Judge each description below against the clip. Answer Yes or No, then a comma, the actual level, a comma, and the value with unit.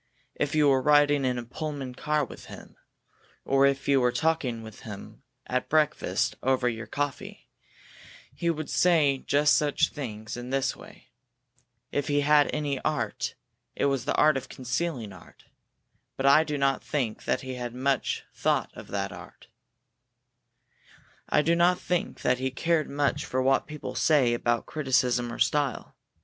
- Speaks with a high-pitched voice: No, low, 135 Hz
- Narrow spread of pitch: No, average, 3.1 semitones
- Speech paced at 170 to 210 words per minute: No, average, 160 wpm